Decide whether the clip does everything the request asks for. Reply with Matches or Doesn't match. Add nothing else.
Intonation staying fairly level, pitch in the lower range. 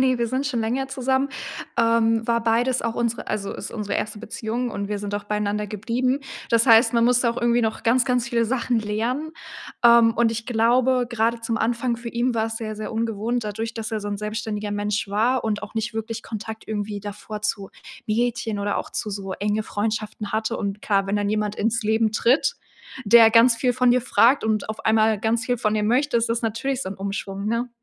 Doesn't match